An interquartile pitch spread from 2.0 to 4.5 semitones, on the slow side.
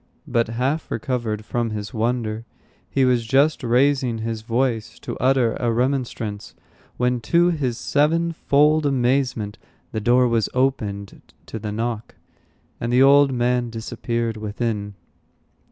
Yes: average, 3.0 semitones; slow, 130 wpm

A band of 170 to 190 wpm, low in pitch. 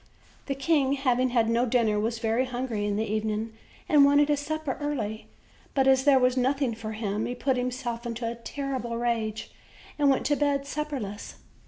No: average, 185 wpm; very high, 250 Hz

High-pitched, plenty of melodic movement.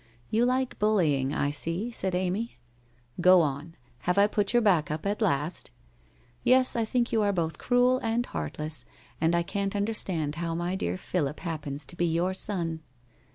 No: medium, 175 Hz; wide, 5.7 semitones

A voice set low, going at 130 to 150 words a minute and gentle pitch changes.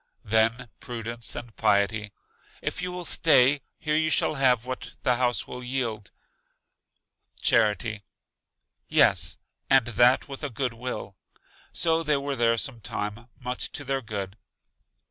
No: low, 125 Hz; average, 140 wpm; average, 3.3 semitones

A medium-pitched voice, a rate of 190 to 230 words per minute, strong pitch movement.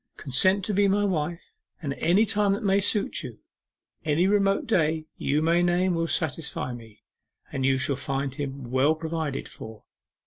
No: medium, 160 Hz; average, 170 wpm; wide, 5.8 semitones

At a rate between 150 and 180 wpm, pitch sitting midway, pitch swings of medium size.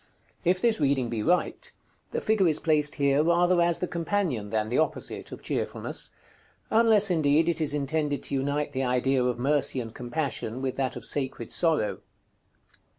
Yes: average, 170 wpm; medium, 145 Hz; average, 4.7 semitones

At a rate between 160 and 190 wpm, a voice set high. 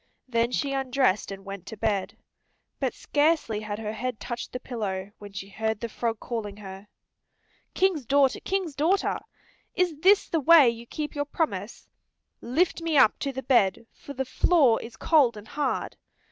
Yes: average, 175 wpm; high, 245 Hz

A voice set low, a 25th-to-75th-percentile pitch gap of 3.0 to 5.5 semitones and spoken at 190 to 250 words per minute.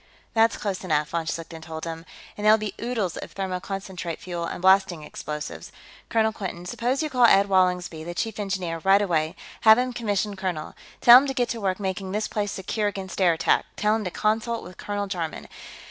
No: high, 195 Hz; average, 3.7 semitones; average, 200 wpm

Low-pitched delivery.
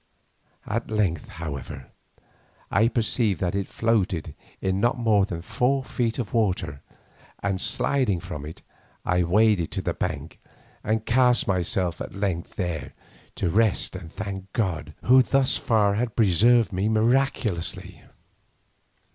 Yes: low, 100 Hz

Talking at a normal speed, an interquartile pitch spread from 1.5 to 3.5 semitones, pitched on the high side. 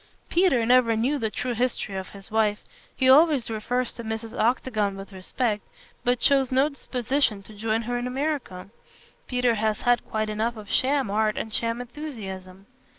Yes: average, 170 wpm; average, 3.1 semitones; high, 230 Hz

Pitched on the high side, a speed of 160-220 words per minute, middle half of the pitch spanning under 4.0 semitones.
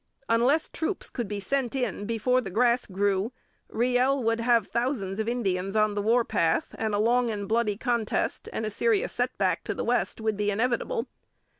Yes: high, 230 Hz; average, 185 wpm; average, 3.3 semitones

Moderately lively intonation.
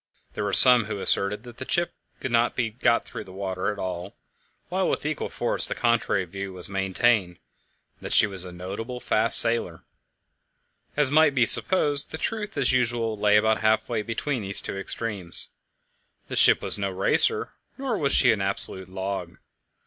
Yes: average, 4.2 semitones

